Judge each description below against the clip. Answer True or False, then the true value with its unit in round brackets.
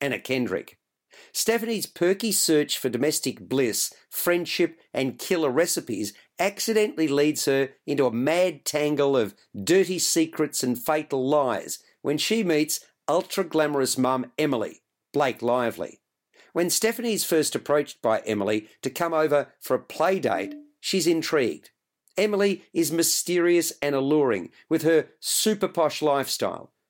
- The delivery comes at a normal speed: False (130 wpm)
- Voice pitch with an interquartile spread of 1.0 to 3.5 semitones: False (4.3 semitones)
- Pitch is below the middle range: False (155 Hz)